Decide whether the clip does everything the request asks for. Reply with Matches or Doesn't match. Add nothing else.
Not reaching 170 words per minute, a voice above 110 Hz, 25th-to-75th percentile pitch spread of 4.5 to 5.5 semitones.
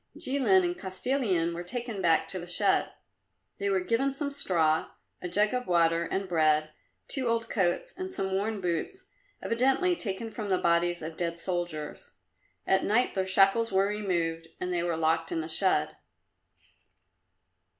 Matches